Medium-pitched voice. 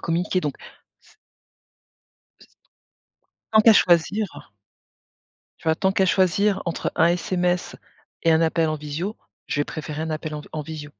Yes: medium, 165 Hz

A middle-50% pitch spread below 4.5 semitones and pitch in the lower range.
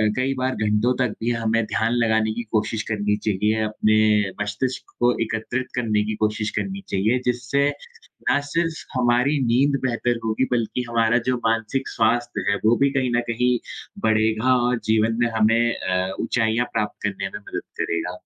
Yes: narrow, 2.5 semitones; low, 115 Hz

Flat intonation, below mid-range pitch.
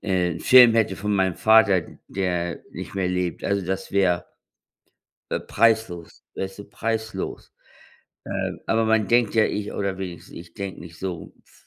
No: average, 3.5 semitones; very low, 95 Hz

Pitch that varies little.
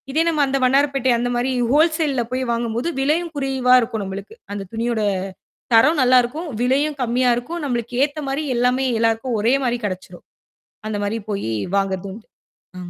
No: average, 3.5 semitones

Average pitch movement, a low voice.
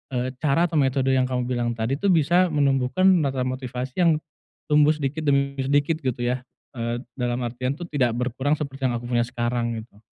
Yes: average, 3.0 semitones; low, 130 Hz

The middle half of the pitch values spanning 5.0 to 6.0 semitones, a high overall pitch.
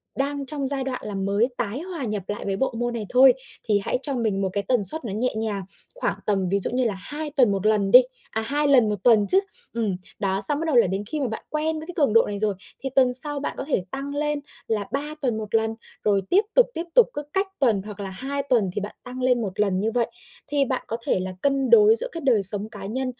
Yes: average, 5.3 semitones; high, 240 Hz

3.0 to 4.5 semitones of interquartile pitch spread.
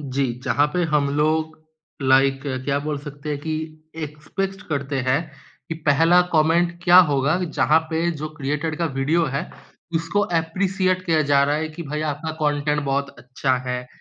No: narrow, 2.5 semitones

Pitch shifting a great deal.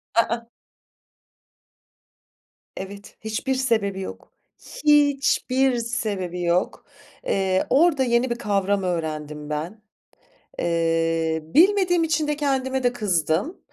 Yes: wide, 7.3 semitones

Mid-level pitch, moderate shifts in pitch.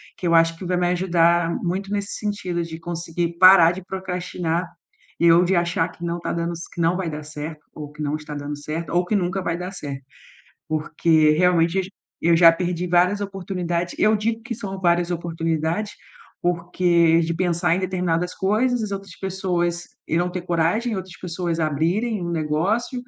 No: medium, 175 Hz; narrow, 2.1 semitones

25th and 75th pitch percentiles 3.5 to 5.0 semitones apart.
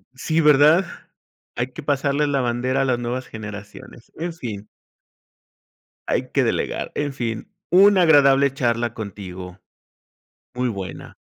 Yes: average, 4.4 semitones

